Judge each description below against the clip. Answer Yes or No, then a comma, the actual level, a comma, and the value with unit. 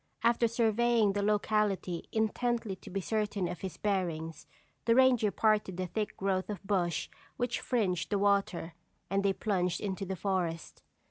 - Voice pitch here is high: Yes, high, 200 Hz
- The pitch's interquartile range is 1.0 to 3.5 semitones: Yes, average, 2.9 semitones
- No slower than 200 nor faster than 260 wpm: No, average, 155 wpm